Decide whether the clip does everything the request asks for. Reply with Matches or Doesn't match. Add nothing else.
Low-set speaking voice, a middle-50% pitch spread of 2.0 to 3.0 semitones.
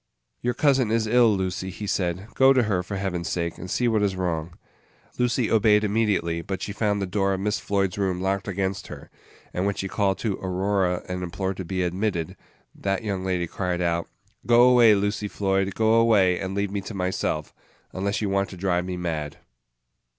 Matches